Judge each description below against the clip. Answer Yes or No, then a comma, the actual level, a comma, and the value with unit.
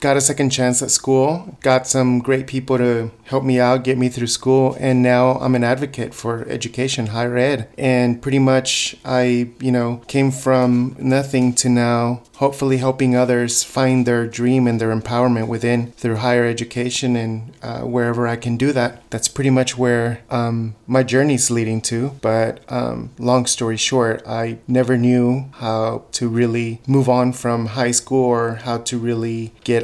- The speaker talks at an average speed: Yes, average, 175 wpm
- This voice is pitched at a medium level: No, low, 125 Hz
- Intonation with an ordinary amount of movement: No, narrow, 1.7 semitones